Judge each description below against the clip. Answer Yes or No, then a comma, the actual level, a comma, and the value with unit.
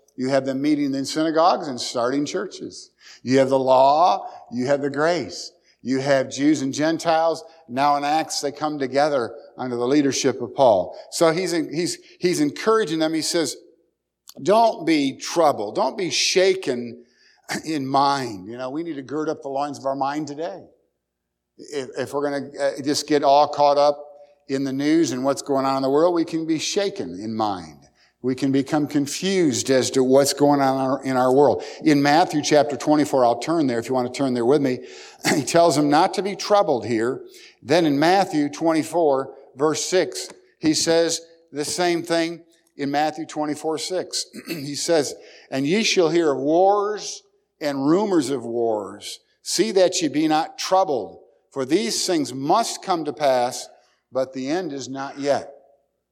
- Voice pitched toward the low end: No, medium, 145 Hz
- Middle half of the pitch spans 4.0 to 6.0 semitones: No, average, 3.6 semitones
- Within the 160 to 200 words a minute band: Yes, average, 180 wpm